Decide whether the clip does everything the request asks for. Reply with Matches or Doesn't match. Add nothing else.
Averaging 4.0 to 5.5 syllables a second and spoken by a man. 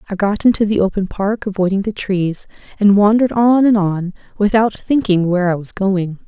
Doesn't match